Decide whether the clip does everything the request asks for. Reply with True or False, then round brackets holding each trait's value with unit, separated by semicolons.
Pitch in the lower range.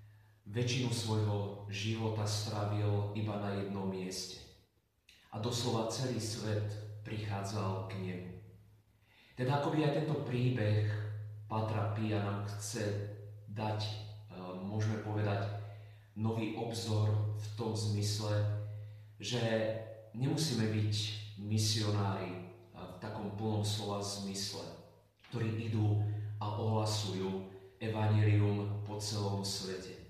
True (105 Hz)